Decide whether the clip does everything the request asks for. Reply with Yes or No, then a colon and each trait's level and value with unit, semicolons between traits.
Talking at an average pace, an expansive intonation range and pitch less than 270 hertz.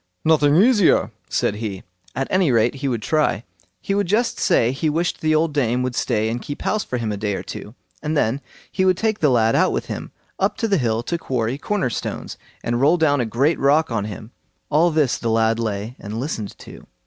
No: fast, 220 wpm; wide, 5.9 semitones; low, 135 Hz